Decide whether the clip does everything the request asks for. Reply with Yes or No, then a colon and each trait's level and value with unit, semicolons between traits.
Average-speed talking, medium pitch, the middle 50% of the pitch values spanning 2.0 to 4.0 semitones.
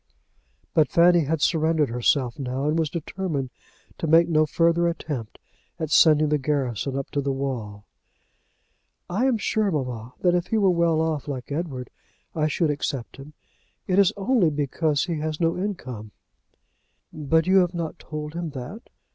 Yes: average, 165 wpm; medium, 155 Hz; average, 3.7 semitones